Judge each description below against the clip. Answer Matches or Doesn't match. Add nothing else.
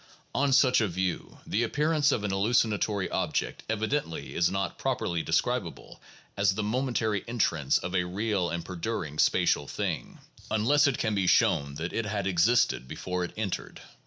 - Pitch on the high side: Doesn't match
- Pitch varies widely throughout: Doesn't match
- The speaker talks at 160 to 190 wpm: Matches